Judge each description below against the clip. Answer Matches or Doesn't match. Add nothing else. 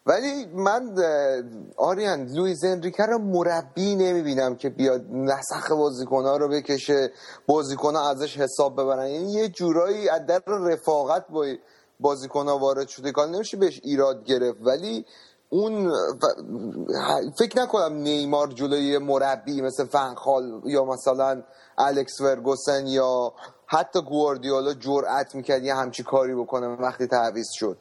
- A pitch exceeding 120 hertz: Matches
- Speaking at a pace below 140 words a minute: Matches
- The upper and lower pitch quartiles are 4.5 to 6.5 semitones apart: Doesn't match